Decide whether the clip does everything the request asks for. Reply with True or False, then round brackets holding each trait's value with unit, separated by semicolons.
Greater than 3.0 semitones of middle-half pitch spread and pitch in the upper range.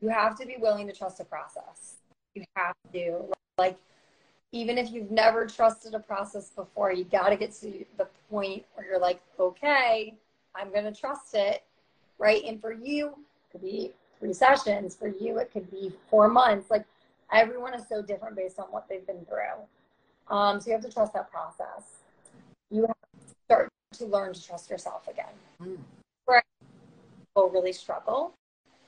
False (2.7 semitones; 210 Hz)